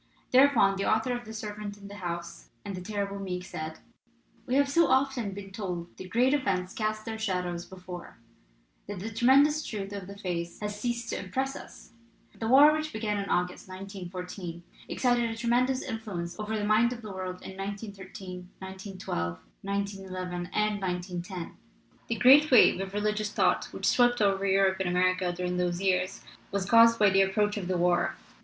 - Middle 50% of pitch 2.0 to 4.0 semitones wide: Yes, average, 3.4 semitones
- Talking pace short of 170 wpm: No, average, 180 wpm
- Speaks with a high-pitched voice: Yes, high, 200 Hz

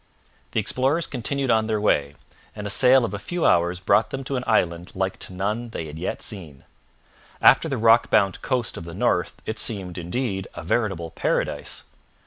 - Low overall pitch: Yes, low, 105 Hz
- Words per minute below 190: No, average, 195 wpm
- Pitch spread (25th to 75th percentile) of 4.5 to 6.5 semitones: Yes, average, 5.2 semitones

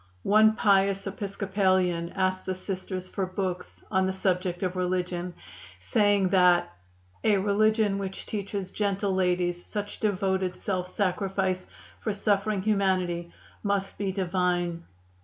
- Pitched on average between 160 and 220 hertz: Yes, high, 190 Hz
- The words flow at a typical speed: No, slow, 120 wpm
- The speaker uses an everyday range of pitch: No, narrow, 1.8 semitones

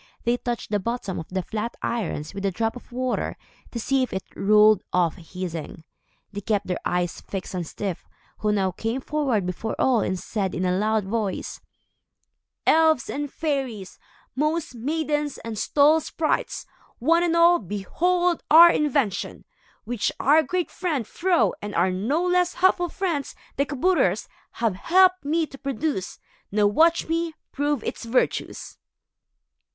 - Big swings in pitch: Yes, wide, 7.7 semitones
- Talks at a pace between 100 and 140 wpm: No, average, 155 wpm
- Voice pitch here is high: Yes, high, 245 Hz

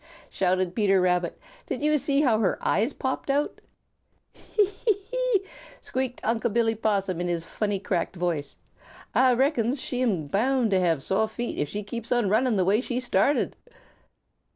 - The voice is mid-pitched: No, high, 225 Hz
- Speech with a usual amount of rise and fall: No, wide, 5.7 semitones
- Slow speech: No, average, 170 wpm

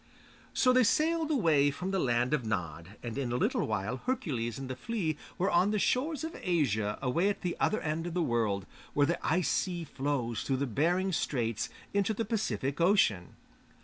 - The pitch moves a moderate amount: No, wide, 8.3 semitones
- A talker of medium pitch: Yes, medium, 150 Hz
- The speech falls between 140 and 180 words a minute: No, average, 190 wpm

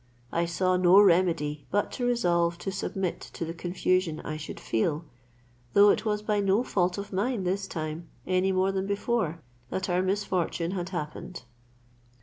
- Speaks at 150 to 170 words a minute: Yes, average, 165 wpm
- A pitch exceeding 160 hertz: Yes, medium, 185 Hz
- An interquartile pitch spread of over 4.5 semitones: No, average, 2.7 semitones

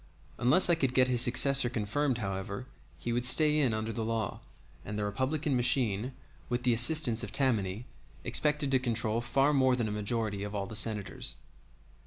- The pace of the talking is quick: No, average, 180 wpm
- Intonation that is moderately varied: Yes, average, 3.7 semitones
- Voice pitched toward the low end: Yes, low, 120 Hz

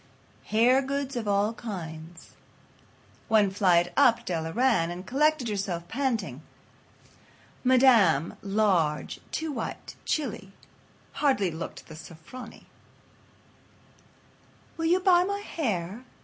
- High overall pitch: Yes, high, 215 Hz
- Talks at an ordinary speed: No, slow, 105 wpm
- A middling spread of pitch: No, wide, 7.1 semitones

